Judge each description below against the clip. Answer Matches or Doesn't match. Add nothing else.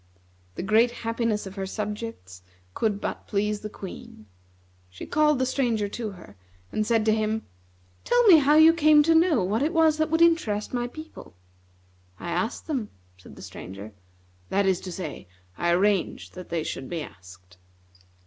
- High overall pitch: Matches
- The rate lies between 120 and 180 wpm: Matches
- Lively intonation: Matches